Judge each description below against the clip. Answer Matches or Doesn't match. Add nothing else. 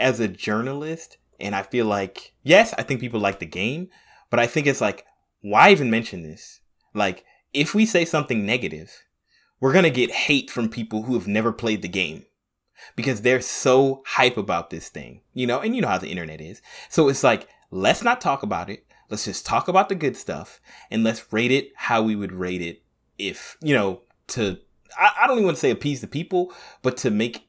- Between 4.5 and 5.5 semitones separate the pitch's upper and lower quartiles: Matches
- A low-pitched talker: Matches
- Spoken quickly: Matches